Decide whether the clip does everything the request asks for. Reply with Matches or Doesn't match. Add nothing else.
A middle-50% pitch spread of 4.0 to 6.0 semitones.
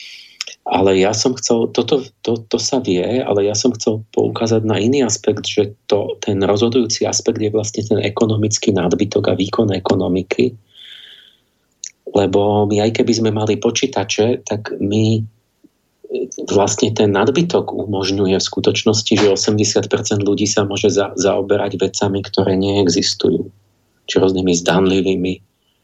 Doesn't match